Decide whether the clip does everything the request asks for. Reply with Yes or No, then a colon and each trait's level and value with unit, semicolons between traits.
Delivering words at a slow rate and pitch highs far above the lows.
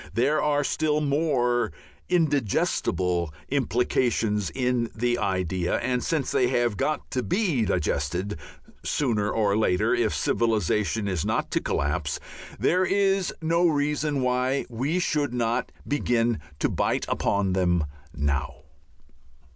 Yes: slow, 125 wpm; wide, 6.3 semitones